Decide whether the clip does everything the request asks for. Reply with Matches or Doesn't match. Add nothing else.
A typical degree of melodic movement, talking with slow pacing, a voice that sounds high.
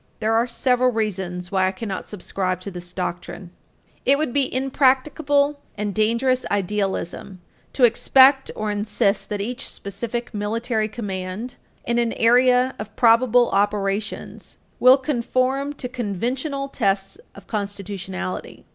Matches